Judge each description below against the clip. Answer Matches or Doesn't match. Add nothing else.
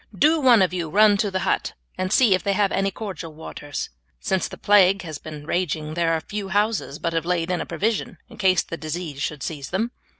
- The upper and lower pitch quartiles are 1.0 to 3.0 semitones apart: Doesn't match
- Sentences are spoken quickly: Matches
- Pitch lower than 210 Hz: Matches